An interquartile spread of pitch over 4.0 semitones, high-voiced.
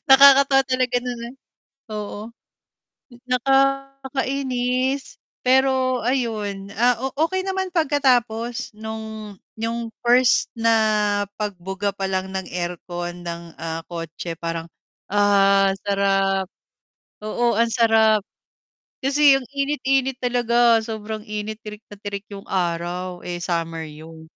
Yes: average, 4.9 semitones; high, 220 Hz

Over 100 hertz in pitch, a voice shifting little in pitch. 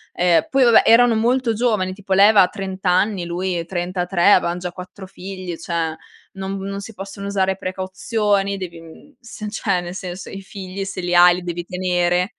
Yes: medium, 185 Hz; narrow, 2.0 semitones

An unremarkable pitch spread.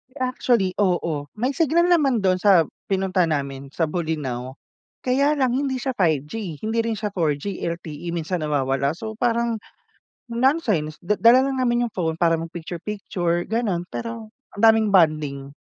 No: wide, 6.6 semitones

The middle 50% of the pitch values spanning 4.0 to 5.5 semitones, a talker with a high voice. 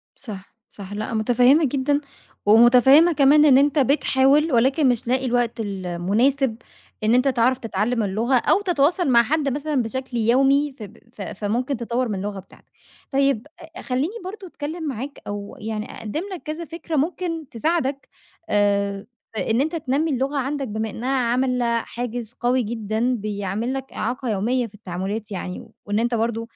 Yes: average, 4.3 semitones; high, 245 Hz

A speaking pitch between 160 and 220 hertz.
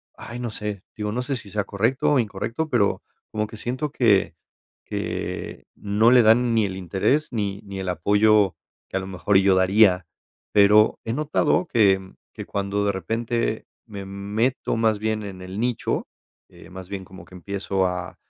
No: low, 105 Hz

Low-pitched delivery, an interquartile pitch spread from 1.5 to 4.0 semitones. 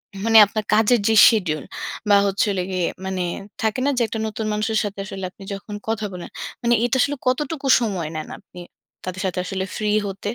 No: high, 210 Hz; average, 2.8 semitones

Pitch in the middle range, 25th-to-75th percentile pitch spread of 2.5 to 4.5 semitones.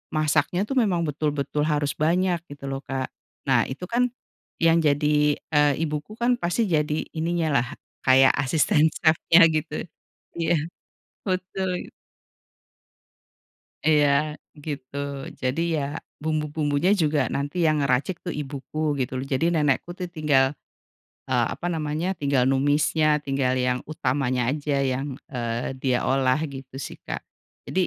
Yes: medium, 150 Hz; average, 3.0 semitones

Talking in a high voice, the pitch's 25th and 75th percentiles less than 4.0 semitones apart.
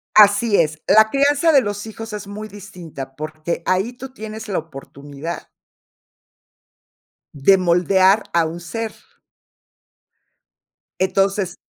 No: high, 195 Hz; average, 4.3 semitones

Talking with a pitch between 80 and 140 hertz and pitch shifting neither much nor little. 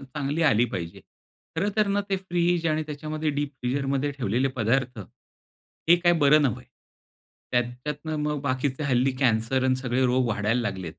Yes: low, 135 Hz; average, 3.8 semitones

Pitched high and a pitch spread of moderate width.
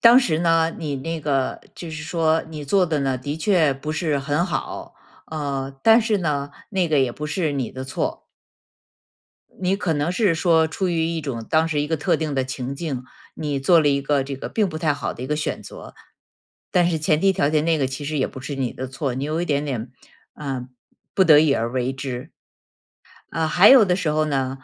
No: medium, 150 Hz; average, 3.3 semitones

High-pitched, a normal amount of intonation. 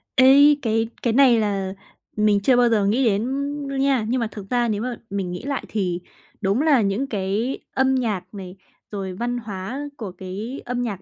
Yes: high, 225 Hz; average, 4.3 semitones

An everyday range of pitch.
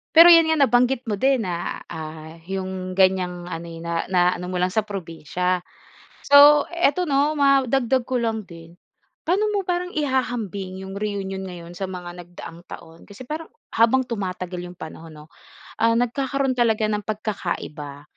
No: wide, 6.7 semitones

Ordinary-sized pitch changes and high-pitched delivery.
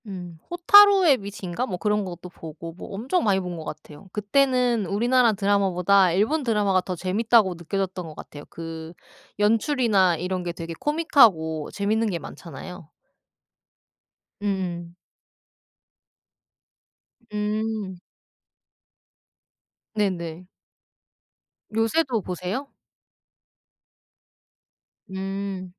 Yes: average, 3.9 semitones; high, 195 Hz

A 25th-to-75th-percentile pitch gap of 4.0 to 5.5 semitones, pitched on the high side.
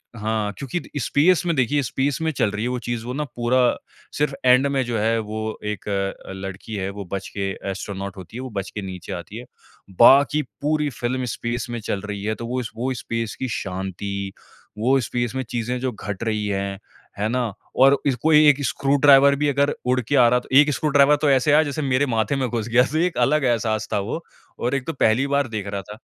No: average, 4.7 semitones; low, 120 Hz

